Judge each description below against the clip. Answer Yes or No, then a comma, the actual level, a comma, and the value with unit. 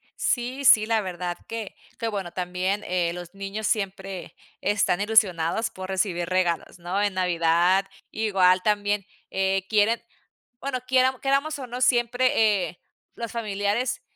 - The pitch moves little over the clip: No, average, 3.8 semitones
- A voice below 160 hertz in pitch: No, high, 200 Hz